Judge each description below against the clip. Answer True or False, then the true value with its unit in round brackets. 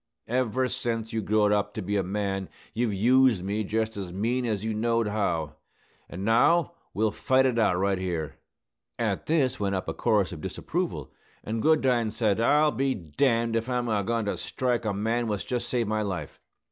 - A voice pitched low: True (110 Hz)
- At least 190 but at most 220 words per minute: True (195 wpm)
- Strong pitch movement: False (3.2 semitones)